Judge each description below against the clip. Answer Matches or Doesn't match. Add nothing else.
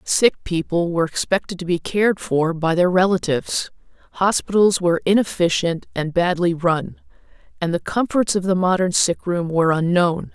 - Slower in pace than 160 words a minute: Matches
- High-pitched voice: Doesn't match